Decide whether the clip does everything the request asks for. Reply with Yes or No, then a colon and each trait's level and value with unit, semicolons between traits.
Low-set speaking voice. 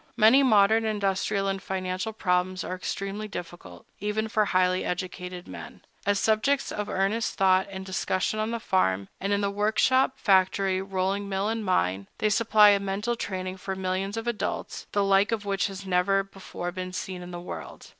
No: high, 195 Hz